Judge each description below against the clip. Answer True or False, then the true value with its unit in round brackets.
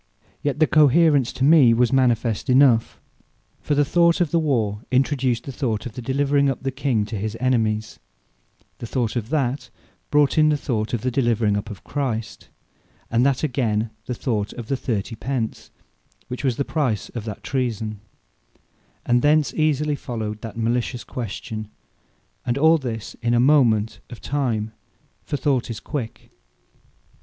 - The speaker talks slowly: False (165 wpm)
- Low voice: True (125 Hz)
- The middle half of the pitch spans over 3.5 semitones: True (3.9 semitones)